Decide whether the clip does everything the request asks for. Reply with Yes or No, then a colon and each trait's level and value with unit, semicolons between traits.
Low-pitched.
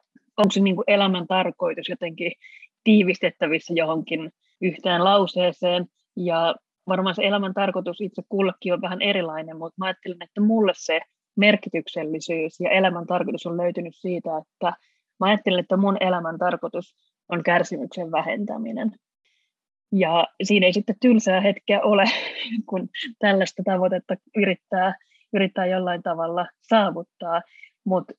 No: medium, 185 Hz